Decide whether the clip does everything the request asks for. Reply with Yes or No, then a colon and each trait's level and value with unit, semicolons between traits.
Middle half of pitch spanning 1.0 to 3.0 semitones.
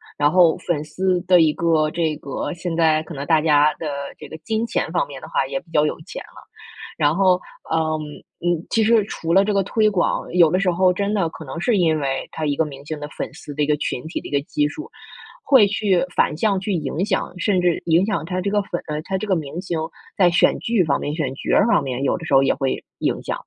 No: average, 3.8 semitones